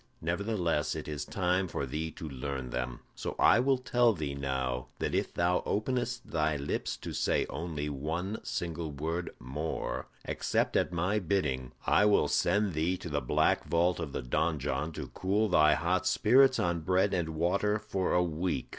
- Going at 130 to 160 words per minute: No, average, 175 wpm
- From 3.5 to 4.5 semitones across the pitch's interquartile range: Yes, average, 4.2 semitones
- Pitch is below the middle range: Yes, very low, 85 Hz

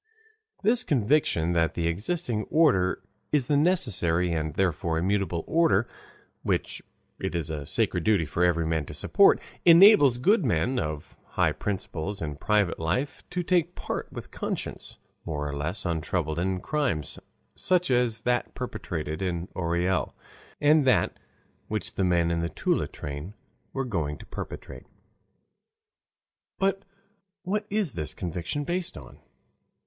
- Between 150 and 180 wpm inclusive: No, average, 140 wpm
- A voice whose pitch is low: Yes, very low, 95 Hz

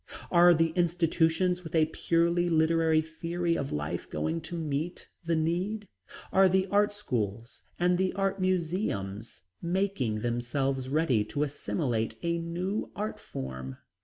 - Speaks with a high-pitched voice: No, medium, 165 Hz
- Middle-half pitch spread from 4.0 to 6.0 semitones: Yes, average, 4.5 semitones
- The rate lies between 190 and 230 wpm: No, slow, 135 wpm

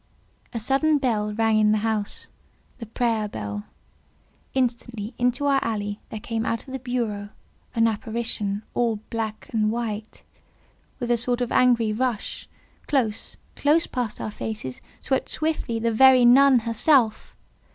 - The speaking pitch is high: Yes, high, 230 Hz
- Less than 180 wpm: Yes, average, 140 wpm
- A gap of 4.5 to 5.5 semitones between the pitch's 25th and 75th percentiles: No, narrow, 2.6 semitones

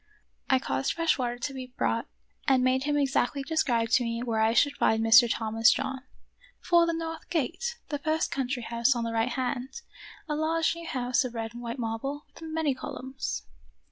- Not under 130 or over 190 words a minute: No, average, 200 wpm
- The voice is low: No, very high, 260 Hz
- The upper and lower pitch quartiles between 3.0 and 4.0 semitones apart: No, average, 4.4 semitones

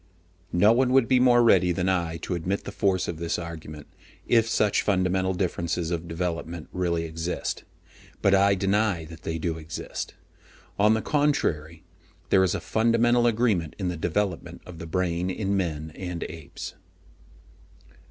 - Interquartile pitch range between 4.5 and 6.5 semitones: No, average, 3.7 semitones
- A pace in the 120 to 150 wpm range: No, average, 160 wpm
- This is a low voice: Yes, very low, 90 Hz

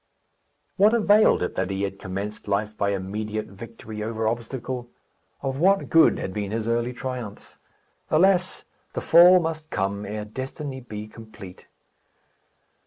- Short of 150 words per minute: Yes, average, 140 wpm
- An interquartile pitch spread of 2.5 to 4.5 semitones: No, average, 5.0 semitones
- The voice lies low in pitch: Yes, low, 110 Hz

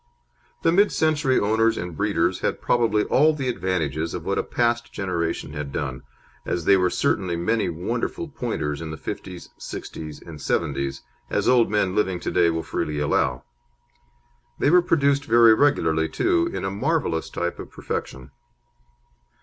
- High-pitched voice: No, very low, 95 Hz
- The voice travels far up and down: Yes, wide, 7.0 semitones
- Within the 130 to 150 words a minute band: No, average, 160 wpm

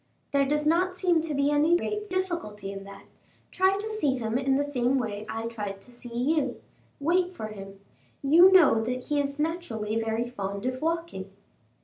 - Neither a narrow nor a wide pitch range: No, wide, 7.0 semitones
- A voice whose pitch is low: No, very high, 275 Hz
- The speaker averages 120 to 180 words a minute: No, average, 190 wpm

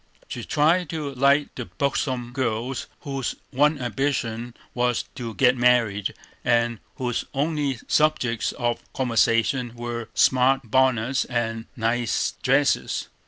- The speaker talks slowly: Yes, slow, 120 wpm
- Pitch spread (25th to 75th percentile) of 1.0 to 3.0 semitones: Yes, narrow, 2.6 semitones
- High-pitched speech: No, low, 125 Hz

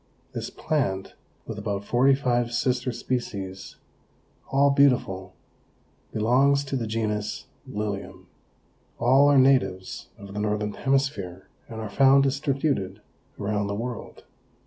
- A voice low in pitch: Yes, low, 120 Hz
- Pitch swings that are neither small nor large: Yes, average, 5.0 semitones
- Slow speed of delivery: Yes, slow, 120 wpm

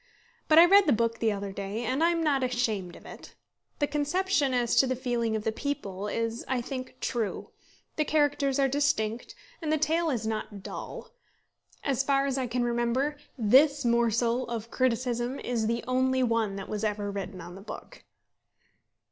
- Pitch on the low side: No, high, 245 Hz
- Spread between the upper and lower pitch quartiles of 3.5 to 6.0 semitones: Yes, average, 4.0 semitones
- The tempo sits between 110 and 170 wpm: No, average, 180 wpm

